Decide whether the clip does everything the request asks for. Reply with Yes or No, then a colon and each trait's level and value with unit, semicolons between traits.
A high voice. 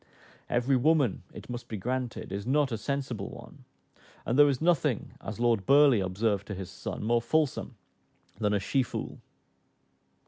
No: low, 120 Hz